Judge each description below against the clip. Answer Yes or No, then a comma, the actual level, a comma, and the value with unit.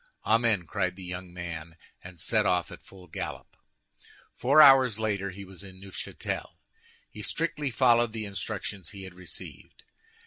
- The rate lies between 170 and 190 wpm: No, average, 150 wpm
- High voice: No, low, 100 Hz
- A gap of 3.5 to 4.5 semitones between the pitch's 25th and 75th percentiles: Yes, average, 4.0 semitones